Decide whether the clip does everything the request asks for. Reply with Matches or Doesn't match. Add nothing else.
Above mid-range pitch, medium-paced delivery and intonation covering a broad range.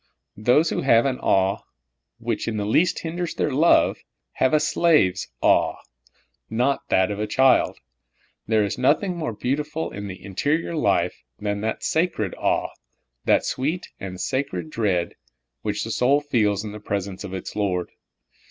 Doesn't match